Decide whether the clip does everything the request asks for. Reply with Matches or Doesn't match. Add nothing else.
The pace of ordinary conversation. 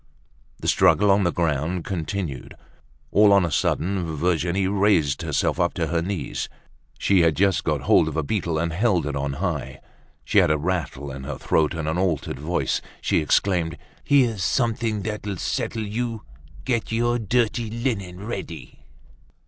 Matches